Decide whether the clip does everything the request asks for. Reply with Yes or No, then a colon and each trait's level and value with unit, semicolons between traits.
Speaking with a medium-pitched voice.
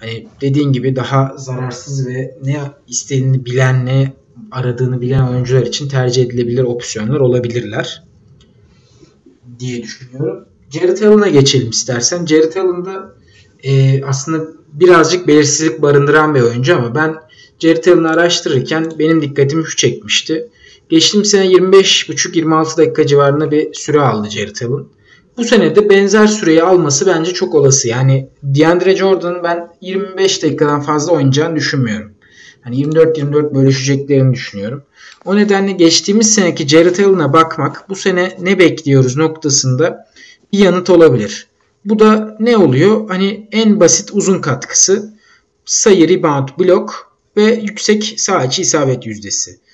Yes: medium, 155 Hz